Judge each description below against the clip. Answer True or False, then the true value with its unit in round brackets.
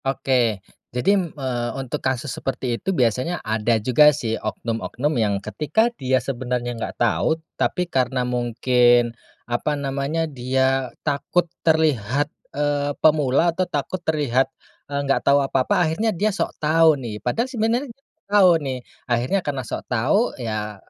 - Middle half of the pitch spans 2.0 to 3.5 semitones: False (4.4 semitones)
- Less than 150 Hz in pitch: True (135 Hz)